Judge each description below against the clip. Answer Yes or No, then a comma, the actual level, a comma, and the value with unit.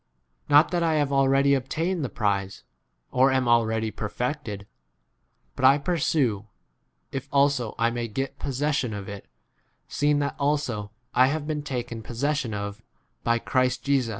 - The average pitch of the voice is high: No, low, 130 Hz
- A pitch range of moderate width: Yes, average, 4.0 semitones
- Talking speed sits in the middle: Yes, average, 160 wpm